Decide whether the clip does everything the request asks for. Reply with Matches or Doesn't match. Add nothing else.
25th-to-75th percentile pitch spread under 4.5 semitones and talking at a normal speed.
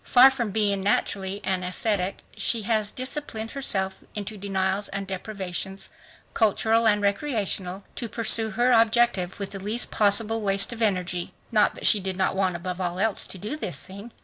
Matches